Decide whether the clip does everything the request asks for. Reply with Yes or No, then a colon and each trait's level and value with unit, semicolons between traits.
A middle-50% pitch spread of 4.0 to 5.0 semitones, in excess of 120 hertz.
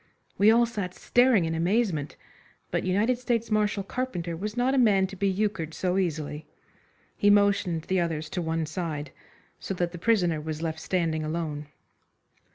Yes: average, 4.5 semitones; medium, 185 Hz